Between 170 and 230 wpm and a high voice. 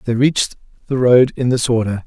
No: fast, 205 wpm; low, 120 Hz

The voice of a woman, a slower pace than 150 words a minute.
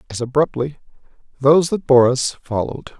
No: male; average, 140 wpm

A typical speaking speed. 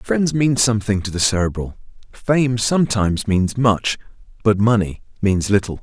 Yes: average, 145 wpm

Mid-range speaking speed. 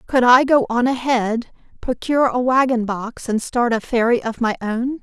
Yes: average, 190 wpm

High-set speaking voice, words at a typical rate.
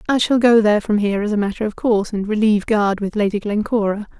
No: high, 210 Hz; fast, 245 wpm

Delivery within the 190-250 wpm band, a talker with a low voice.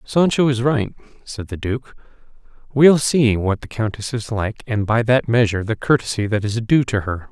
Yes: average, 195 wpm; low, 115 Hz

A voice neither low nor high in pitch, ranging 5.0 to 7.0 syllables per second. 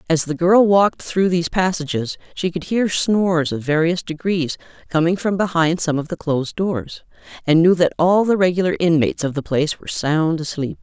Yes: medium, 170 Hz; 5.4 syllables/s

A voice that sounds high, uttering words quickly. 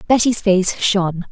No: high, 195 Hz; slow, 135 wpm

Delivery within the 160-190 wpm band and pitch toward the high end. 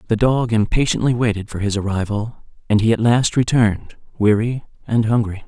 No: average, 165 wpm; low, 110 Hz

